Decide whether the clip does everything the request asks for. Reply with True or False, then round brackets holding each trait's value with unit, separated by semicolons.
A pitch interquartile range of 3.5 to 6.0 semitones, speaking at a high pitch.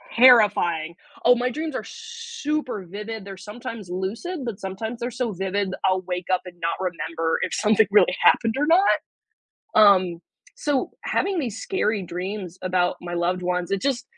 True (5.3 semitones; 205 Hz)